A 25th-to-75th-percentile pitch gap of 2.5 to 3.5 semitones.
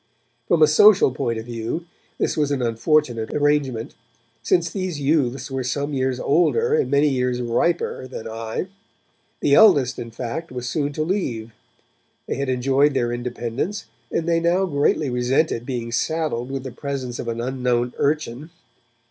No: average, 4.2 semitones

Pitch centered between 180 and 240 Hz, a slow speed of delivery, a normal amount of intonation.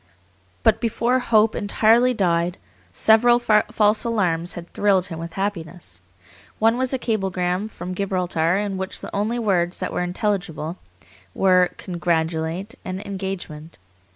Yes: high, 190 Hz; slow, 130 wpm; average, 3.7 semitones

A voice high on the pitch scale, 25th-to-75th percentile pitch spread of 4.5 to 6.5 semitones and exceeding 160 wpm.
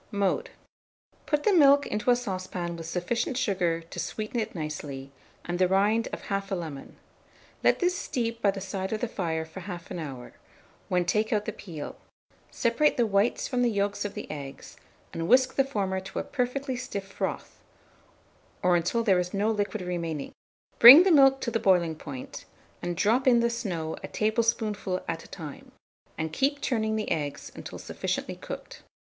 Yes: high, 200 Hz; average, 5.2 semitones; average, 180 wpm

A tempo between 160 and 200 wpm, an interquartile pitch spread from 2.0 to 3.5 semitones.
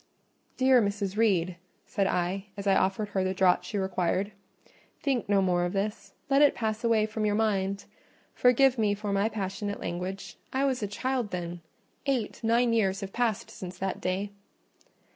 Yes: average, 180 wpm; average, 2.9 semitones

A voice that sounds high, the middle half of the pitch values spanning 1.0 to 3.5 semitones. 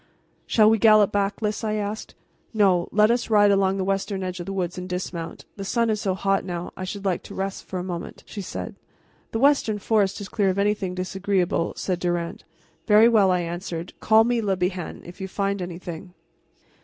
Yes: high, 195 Hz; narrow, 2.5 semitones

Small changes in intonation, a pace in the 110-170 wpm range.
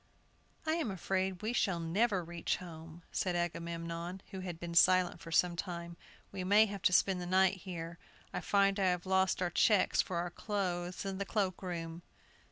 No: narrow, 2.1 semitones; average, 185 wpm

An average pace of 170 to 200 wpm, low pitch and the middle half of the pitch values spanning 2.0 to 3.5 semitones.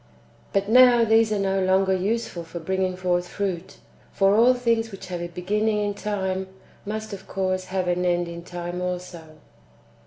No: average, 175 wpm; high, 190 Hz; average, 2.8 semitones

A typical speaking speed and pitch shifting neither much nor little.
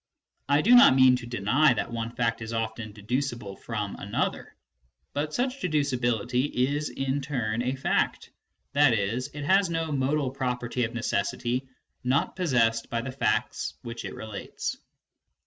Yes: average, 150 wpm; average, 3.7 semitones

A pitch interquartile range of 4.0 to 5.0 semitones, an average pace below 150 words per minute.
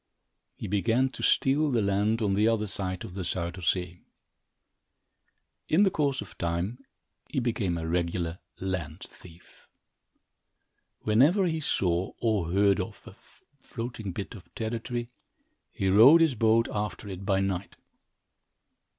Yes: average, 4.4 semitones; average, 140 wpm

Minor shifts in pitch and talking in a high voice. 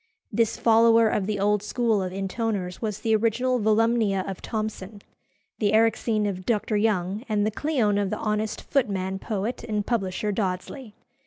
Yes: narrow, 2.3 semitones; high, 215 Hz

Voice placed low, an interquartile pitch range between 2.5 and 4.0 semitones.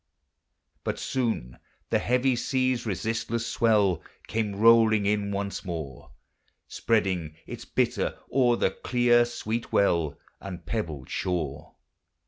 No: low, 105 Hz; average, 4.7 semitones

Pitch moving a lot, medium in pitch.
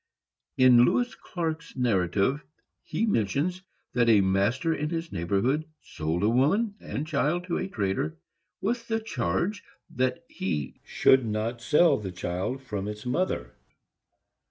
No: wide, 8.7 semitones; low, 125 Hz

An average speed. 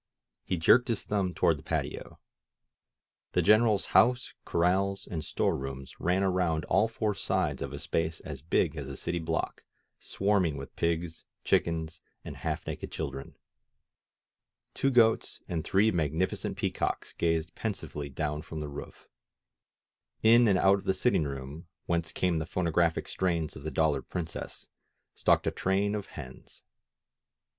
Yes: average, 150 wpm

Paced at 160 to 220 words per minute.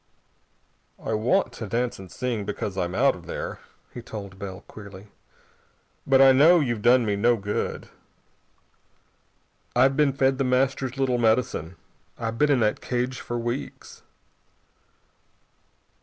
No: average, 140 wpm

